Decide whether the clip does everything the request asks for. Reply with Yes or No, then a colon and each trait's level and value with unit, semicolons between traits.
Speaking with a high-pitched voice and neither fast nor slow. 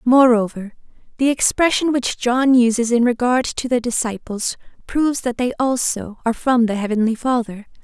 Yes: high, 240 Hz; average, 155 wpm